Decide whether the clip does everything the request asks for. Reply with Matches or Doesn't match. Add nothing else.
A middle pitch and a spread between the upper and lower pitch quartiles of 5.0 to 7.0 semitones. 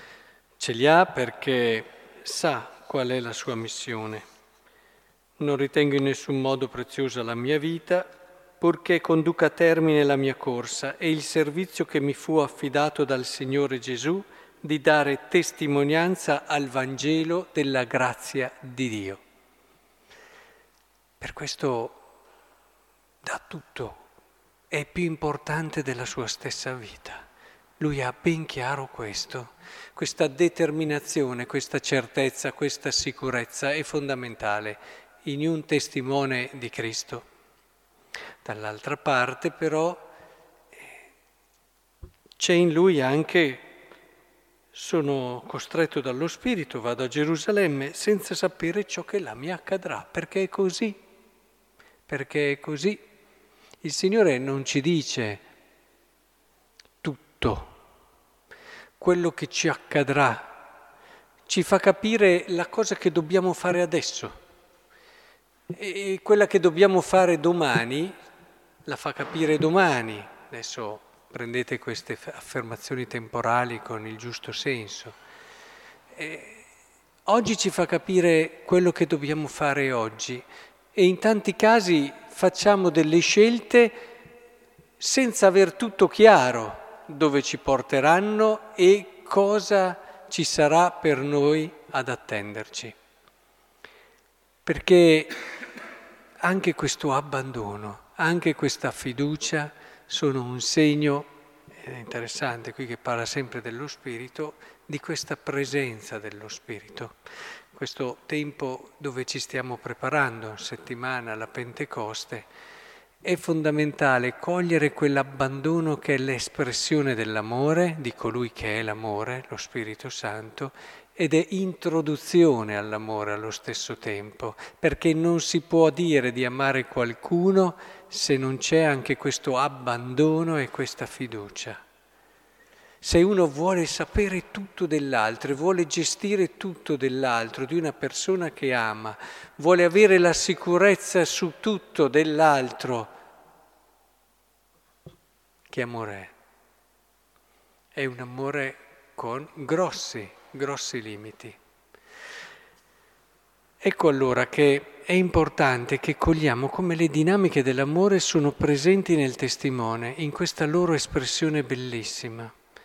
Matches